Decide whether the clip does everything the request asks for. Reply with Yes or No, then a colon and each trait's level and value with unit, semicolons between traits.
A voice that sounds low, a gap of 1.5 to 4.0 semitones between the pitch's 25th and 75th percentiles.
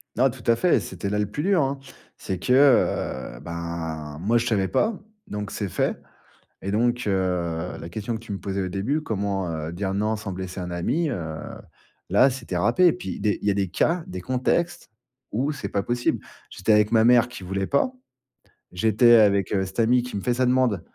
No: low, 105 Hz; average, 4.6 semitones